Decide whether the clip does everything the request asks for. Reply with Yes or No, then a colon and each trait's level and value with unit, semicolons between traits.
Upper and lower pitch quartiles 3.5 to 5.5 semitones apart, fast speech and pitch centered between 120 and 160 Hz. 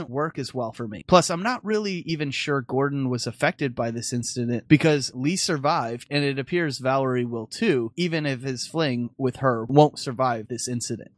No: average, 4.0 semitones; average, 195 wpm; low, 135 Hz